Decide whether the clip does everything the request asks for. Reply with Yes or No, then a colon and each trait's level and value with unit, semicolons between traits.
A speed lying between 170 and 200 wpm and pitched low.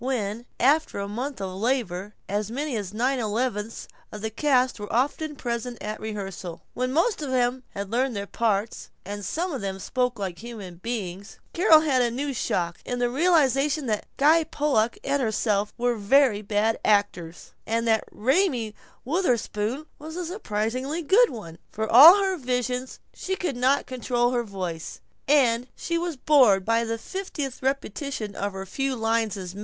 No: average, 175 wpm; high, 240 Hz